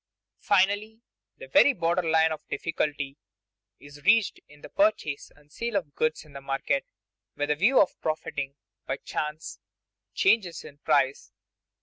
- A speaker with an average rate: Yes, average, 145 wpm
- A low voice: No, medium, 160 Hz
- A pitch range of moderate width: No, wide, 5.9 semitones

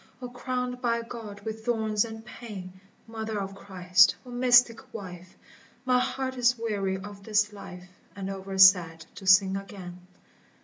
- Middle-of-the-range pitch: No, high, 210 Hz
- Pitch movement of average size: Yes, average, 3.6 semitones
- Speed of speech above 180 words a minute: No, average, 150 wpm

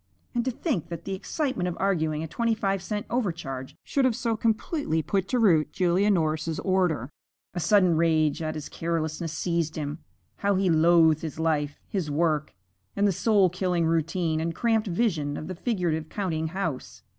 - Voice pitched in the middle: Yes, medium, 170 Hz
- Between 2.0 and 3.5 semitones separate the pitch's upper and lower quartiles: No, average, 3.9 semitones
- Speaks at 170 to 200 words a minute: Yes, average, 180 wpm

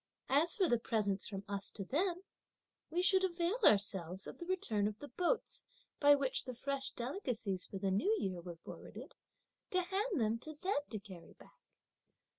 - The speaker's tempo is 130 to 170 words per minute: No, average, 180 wpm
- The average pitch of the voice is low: No, very high, 255 Hz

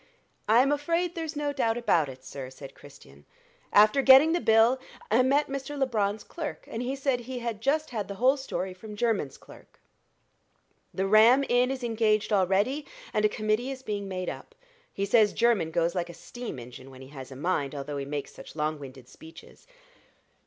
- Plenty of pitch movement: Yes, wide, 8.1 semitones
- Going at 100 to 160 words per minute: No, average, 190 wpm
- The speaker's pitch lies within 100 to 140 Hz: No, high, 215 Hz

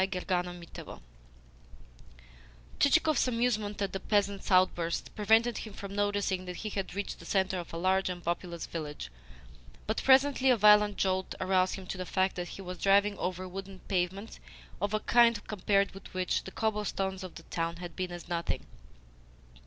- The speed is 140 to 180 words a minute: Yes, average, 170 wpm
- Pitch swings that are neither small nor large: No, narrow, 2.3 semitones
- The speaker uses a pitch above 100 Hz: Yes, high, 190 Hz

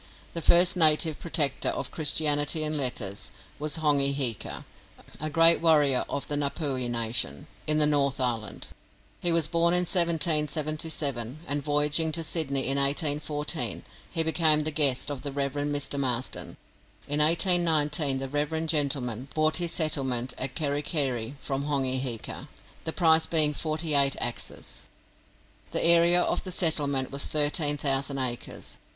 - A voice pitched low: No, medium, 145 Hz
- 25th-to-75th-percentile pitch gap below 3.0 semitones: Yes, narrow, 2.6 semitones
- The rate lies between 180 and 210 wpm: No, average, 145 wpm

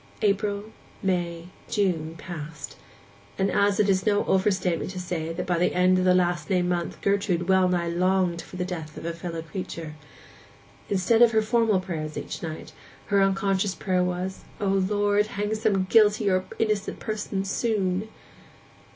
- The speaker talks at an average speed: Yes, average, 160 wpm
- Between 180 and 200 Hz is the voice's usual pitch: Yes, medium, 185 Hz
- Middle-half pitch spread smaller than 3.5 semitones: Yes, narrow, 2.5 semitones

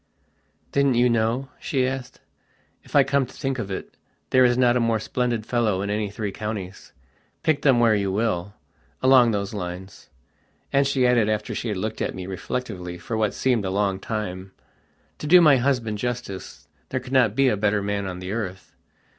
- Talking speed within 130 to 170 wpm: No, average, 190 wpm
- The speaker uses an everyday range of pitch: Yes, average, 4.1 semitones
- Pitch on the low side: Yes, low, 110 Hz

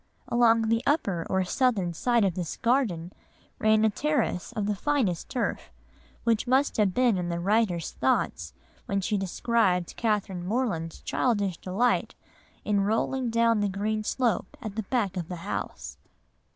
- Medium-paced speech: Yes, average, 155 wpm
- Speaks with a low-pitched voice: No, high, 210 Hz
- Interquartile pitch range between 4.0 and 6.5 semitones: Yes, average, 4.3 semitones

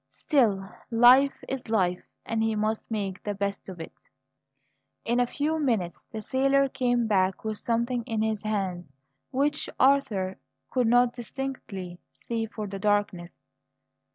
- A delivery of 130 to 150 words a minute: Yes, average, 145 wpm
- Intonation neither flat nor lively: Yes, average, 4.0 semitones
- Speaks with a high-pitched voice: Yes, high, 220 Hz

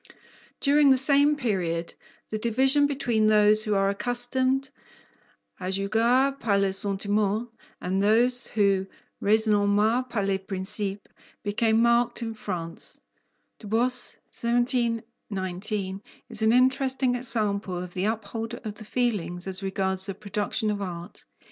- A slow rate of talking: Yes, slow, 130 wpm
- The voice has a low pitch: No, high, 215 Hz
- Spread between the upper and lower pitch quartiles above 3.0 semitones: Yes, average, 3.7 semitones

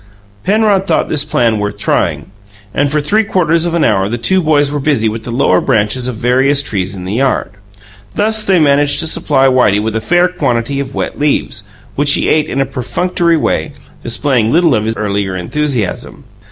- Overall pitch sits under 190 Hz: Yes, low, 135 Hz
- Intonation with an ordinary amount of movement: No, wide, 5.9 semitones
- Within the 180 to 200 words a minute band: Yes, average, 195 wpm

